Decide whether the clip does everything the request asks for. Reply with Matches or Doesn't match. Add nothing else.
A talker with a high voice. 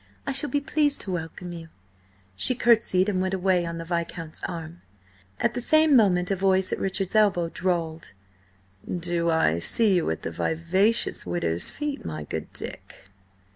Doesn't match